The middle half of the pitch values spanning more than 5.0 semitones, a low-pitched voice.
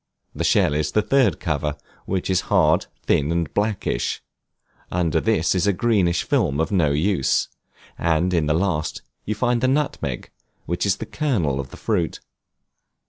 Yes: wide, 5.4 semitones; very low, 90 Hz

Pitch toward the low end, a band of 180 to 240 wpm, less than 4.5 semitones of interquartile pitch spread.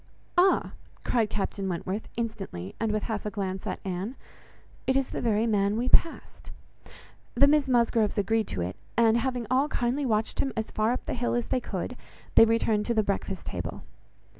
No: high, 225 Hz; average, 190 wpm; average, 3.3 semitones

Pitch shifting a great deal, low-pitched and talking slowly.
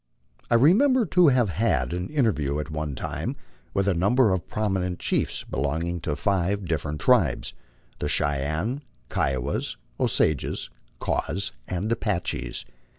Yes: wide, 7.0 semitones; very low, 90 Hz; slow, 130 wpm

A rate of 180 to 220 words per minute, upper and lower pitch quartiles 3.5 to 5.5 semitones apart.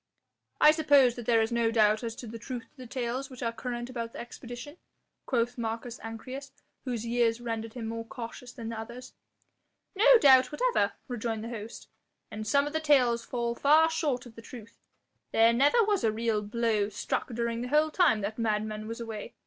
No: average, 195 wpm; narrow, 2.4 semitones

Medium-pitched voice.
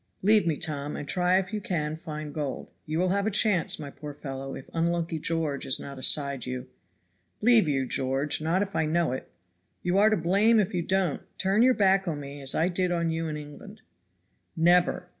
Yes: medium, 165 Hz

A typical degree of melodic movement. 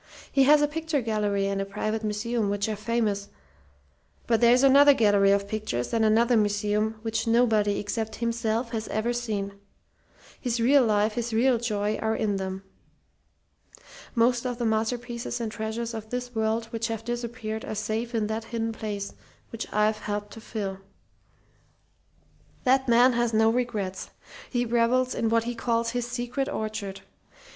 No: narrow, 2.1 semitones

